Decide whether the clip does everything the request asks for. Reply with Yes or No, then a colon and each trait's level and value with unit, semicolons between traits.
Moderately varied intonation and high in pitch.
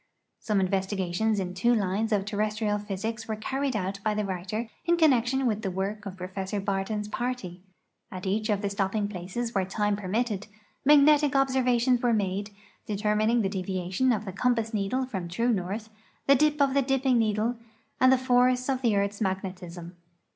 Yes: average, 4.1 semitones; high, 210 Hz